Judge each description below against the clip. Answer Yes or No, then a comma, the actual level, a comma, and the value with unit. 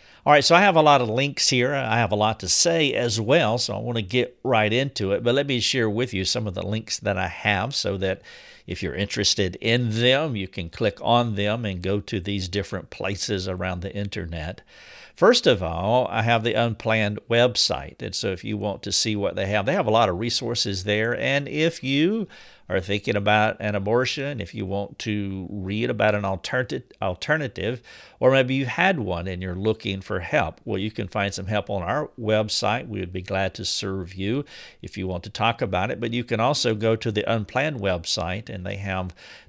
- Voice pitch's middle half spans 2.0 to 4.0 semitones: Yes, average, 3.6 semitones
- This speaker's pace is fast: Yes, fast, 225 wpm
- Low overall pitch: Yes, low, 105 Hz